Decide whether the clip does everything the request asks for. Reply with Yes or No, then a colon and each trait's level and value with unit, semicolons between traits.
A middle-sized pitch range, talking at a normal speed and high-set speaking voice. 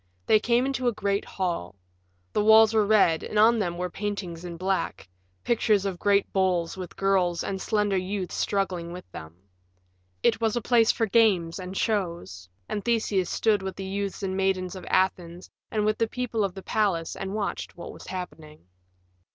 Yes: average, 3.1 semitones; average, 185 wpm; high, 195 Hz